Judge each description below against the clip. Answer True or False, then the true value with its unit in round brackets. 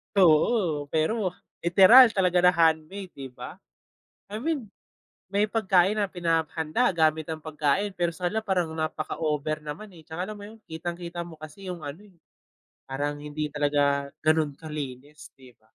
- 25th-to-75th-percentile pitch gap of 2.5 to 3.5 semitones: False (3.9 semitones)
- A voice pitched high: False (165 Hz)